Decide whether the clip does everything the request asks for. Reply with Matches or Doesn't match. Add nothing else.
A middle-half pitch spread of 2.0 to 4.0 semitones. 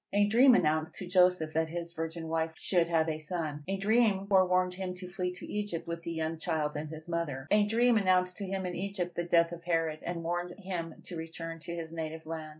Matches